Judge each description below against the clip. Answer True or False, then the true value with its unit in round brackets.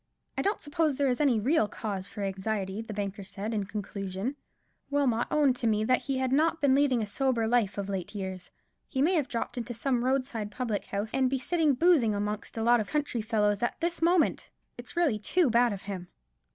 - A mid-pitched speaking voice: False (235 Hz)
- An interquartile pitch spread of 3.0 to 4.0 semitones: False (5.0 semitones)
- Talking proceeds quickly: True (215 wpm)